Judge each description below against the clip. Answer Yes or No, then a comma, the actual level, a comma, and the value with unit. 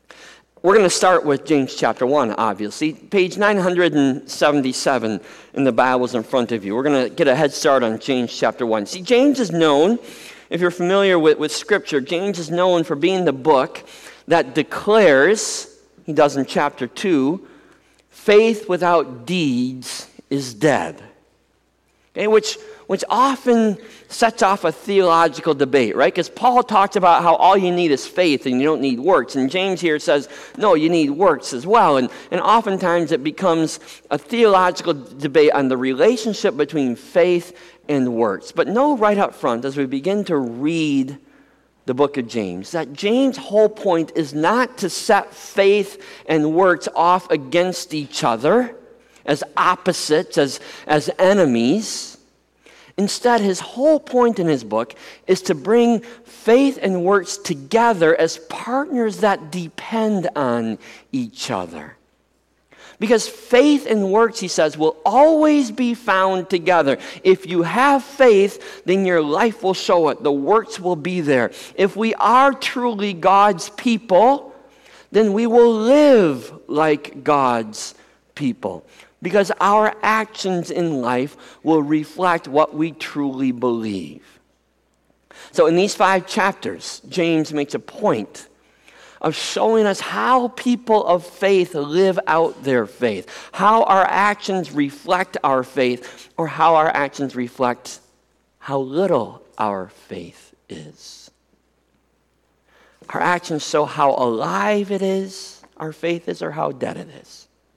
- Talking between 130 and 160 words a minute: Yes, average, 150 wpm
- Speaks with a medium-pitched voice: Yes, medium, 180 Hz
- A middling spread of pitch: No, wide, 6.5 semitones